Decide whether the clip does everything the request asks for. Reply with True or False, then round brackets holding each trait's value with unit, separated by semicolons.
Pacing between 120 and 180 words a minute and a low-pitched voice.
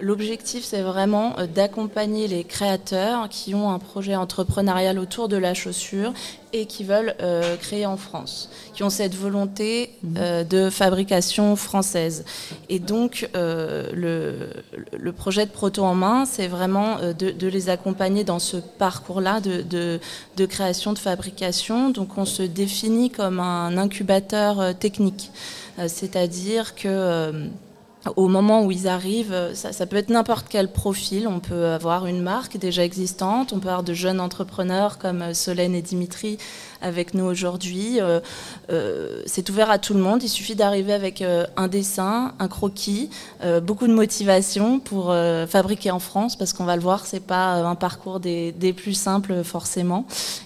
False (165 wpm; 190 Hz)